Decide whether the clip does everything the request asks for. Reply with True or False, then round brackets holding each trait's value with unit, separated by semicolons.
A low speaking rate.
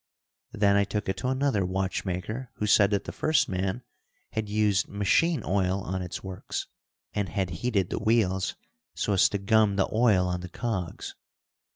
False (175 wpm)